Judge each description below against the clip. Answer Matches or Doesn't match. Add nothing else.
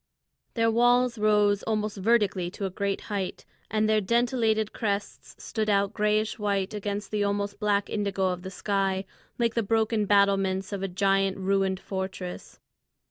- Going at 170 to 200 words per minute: Doesn't match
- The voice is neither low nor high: Doesn't match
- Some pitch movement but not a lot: Doesn't match